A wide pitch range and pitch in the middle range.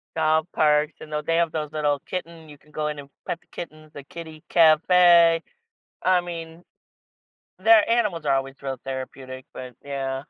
No: average, 2.9 semitones; medium, 155 Hz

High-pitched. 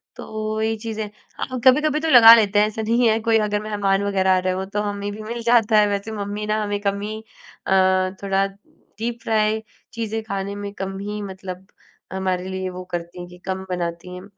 Yes: high, 205 Hz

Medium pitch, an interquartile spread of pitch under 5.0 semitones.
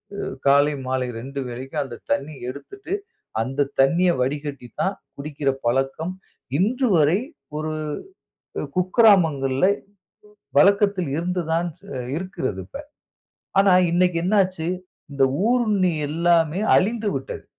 No: medium, 165 Hz; average, 5.3 semitones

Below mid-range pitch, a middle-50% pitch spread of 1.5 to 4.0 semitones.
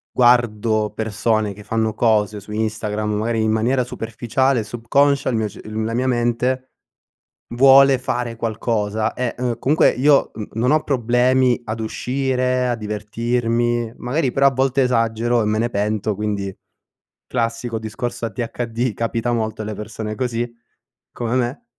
Yes: low, 115 Hz; narrow, 2.5 semitones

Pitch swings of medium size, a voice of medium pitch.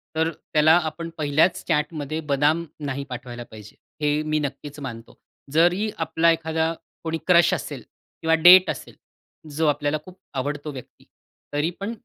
No: narrow, 2.2 semitones; medium, 155 Hz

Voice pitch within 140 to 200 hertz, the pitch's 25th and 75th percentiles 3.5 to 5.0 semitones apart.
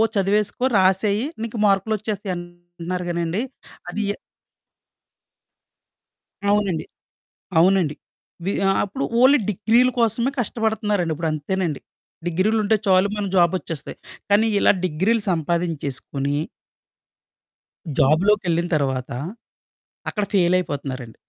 Yes: medium, 185 Hz; average, 3.8 semitones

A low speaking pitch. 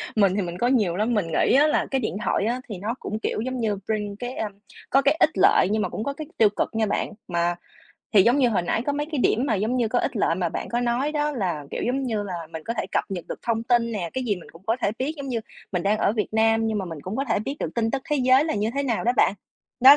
No: high, 225 Hz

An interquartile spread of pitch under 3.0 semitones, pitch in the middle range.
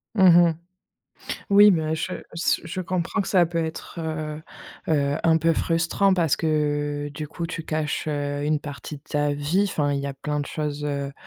Yes: narrow, 2.4 semitones; medium, 155 Hz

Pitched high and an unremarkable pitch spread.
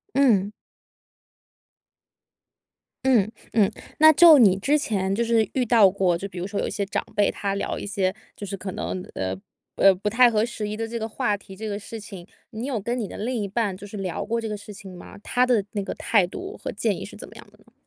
Yes: high, 210 Hz; average, 3.1 semitones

